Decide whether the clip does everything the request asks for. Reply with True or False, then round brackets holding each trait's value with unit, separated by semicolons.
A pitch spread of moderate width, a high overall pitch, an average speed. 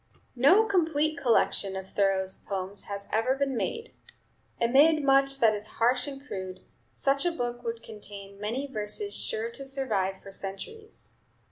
False (6.0 semitones; 245 Hz; 150 wpm)